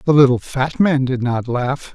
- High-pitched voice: No, low, 135 Hz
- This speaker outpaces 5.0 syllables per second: No, 4.4 syllables/s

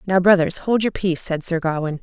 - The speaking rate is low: No, fast, 235 wpm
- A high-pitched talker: No, medium, 180 Hz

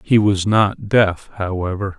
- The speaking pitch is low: Yes, low, 100 Hz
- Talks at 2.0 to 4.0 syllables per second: Yes, 3.9 syllables/s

